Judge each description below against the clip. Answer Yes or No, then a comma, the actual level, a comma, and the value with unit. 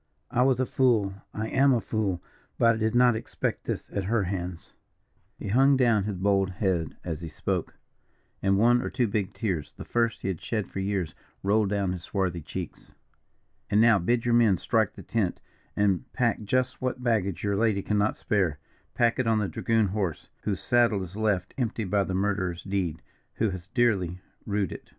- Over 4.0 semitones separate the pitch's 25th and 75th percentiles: No, average, 3.5 semitones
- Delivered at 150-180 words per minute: No, average, 195 wpm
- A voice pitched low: Yes, low, 105 Hz